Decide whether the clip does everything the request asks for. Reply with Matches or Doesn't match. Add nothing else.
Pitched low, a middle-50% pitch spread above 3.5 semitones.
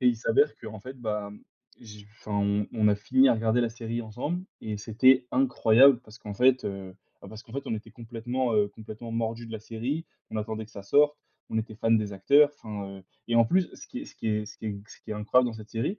Doesn't match